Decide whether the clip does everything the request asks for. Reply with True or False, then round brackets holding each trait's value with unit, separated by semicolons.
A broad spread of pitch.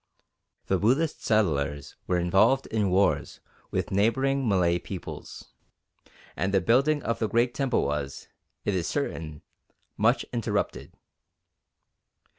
True (5.8 semitones)